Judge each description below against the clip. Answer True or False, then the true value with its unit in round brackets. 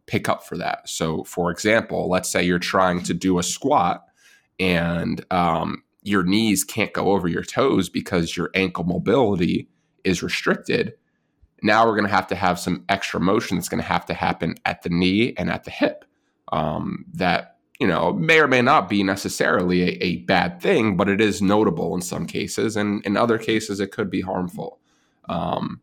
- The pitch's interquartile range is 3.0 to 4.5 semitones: False (2.4 semitones)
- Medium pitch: False (95 Hz)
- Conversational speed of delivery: True (195 wpm)